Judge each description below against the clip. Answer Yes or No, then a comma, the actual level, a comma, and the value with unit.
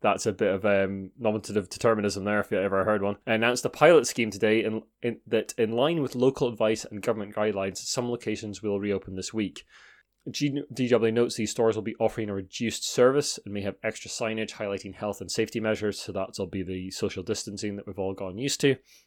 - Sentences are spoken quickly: Yes, fast, 215 wpm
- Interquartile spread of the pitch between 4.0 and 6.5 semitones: No, narrow, 2.5 semitones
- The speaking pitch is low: Yes, low, 110 Hz